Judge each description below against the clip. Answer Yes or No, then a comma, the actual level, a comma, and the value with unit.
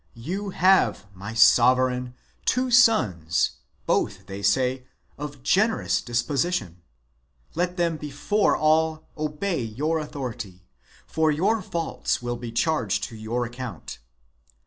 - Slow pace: Yes, slow, 115 wpm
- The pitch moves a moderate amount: No, wide, 6.4 semitones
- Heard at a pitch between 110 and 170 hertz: Yes, low, 135 Hz